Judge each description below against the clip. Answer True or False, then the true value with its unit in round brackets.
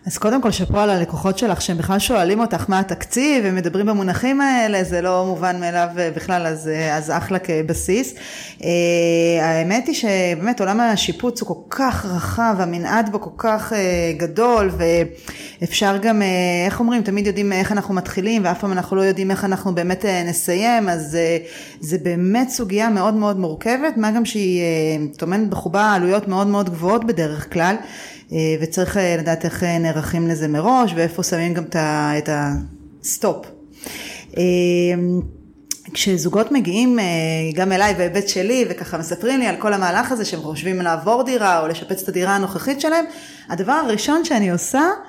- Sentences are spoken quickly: True (155 wpm)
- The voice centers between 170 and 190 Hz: True (185 Hz)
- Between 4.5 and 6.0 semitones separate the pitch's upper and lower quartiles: False (4.1 semitones)